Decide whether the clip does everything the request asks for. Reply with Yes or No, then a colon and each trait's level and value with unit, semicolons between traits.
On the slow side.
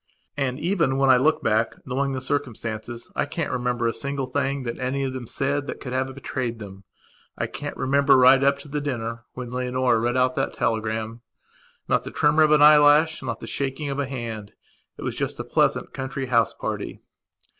No: average, 195 wpm